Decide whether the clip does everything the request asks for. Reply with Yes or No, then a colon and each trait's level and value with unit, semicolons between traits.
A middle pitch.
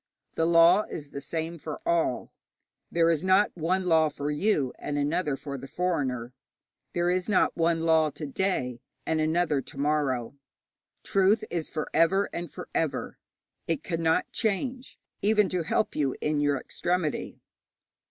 Yes: medium, 165 Hz